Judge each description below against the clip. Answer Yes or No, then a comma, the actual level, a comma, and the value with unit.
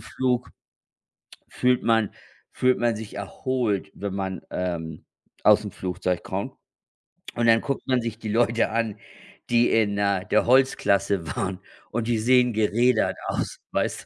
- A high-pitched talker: No, low, 110 Hz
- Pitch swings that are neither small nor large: Yes, average, 3.3 semitones